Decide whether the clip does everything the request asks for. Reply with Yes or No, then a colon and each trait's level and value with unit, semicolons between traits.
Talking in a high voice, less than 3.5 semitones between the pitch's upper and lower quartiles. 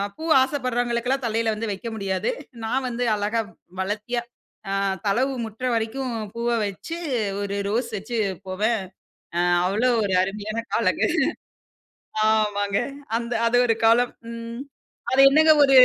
Yes: high, 230 Hz; average, 3.0 semitones